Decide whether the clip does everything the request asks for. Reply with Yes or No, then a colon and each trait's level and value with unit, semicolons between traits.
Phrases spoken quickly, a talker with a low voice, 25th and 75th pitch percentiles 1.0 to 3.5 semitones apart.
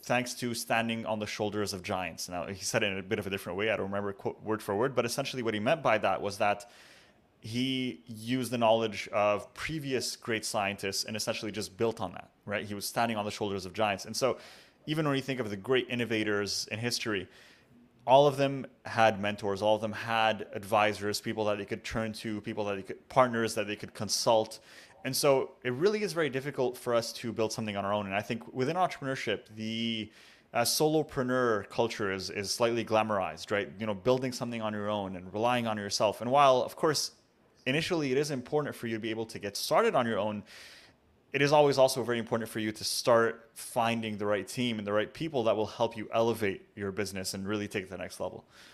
Yes: fast, 230 wpm; low, 110 Hz; average, 3.1 semitones